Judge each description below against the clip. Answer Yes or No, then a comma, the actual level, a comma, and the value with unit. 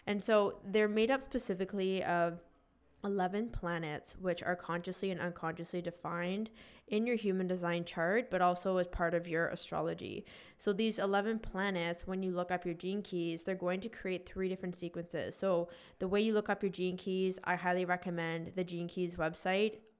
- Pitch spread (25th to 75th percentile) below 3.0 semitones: Yes, narrow, 2.6 semitones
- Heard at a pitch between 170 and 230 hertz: Yes, medium, 185 Hz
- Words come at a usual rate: Yes, average, 185 wpm